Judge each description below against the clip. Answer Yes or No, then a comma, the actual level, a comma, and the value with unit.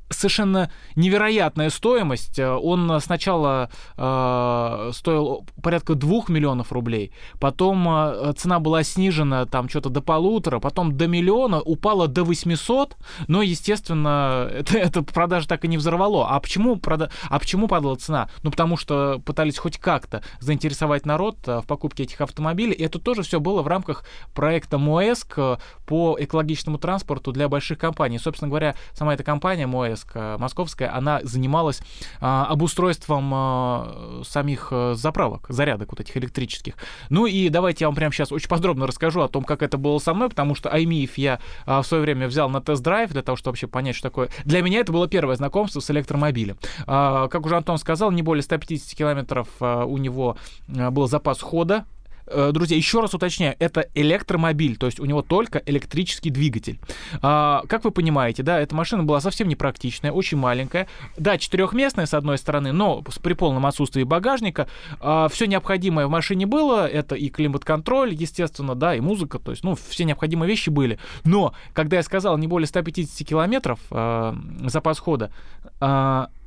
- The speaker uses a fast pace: Yes, fast, 165 wpm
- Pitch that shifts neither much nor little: Yes, average, 4.0 semitones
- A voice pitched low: No, medium, 155 Hz